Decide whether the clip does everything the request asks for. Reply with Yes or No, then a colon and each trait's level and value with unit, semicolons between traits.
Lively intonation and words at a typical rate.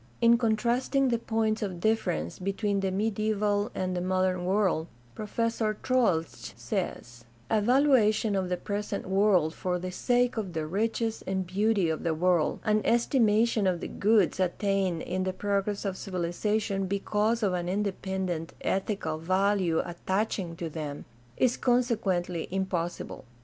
No: average, 3.3 semitones; average, 145 wpm